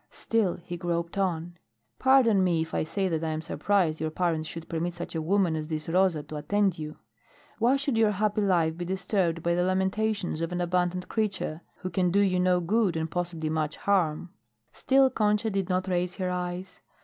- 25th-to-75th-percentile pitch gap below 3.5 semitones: Yes, average, 3.1 semitones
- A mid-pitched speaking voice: Yes, medium, 180 Hz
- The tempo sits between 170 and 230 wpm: Yes, average, 200 wpm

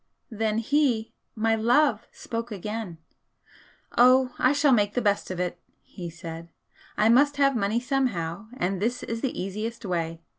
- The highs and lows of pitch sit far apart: No, average, 4.8 semitones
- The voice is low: No, high, 225 Hz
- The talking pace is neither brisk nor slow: Yes, average, 155 wpm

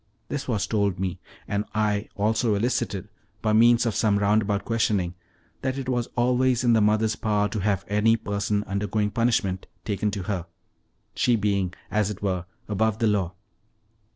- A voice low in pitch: Yes, low, 105 Hz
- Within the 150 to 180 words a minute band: Yes, average, 170 wpm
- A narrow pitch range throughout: Yes, narrow, 2.1 semitones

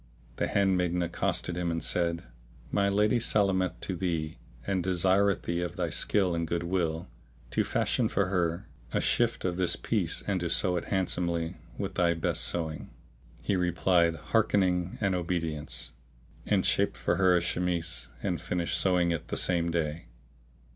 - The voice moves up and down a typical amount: No, narrow, 1.8 semitones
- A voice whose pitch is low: Yes, very low, 90 Hz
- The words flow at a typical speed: Yes, average, 160 wpm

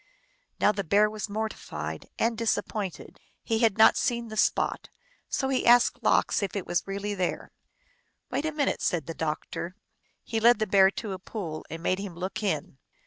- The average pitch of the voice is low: No, high, 205 Hz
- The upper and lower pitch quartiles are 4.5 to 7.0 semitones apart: No, average, 3.4 semitones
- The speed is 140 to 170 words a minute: No, average, 190 wpm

